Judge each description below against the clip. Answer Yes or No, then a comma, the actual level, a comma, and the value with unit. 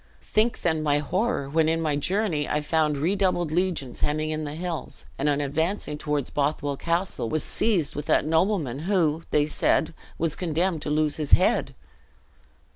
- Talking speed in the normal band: Yes, average, 170 wpm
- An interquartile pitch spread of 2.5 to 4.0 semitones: Yes, average, 2.9 semitones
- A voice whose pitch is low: No, medium, 155 Hz